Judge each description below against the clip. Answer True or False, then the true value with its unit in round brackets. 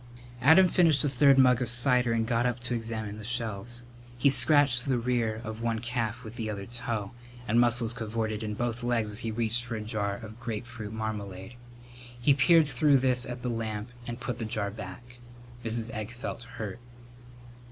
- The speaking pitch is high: False (120 Hz)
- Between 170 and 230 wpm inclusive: True (190 wpm)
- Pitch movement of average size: False (2.1 semitones)